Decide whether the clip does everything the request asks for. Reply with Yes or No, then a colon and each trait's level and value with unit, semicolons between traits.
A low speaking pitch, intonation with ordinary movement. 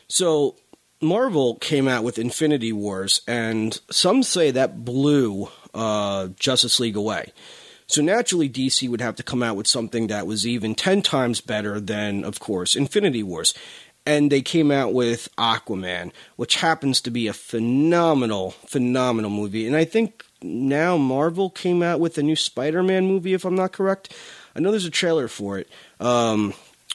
No: low, 125 Hz; wide, 6.7 semitones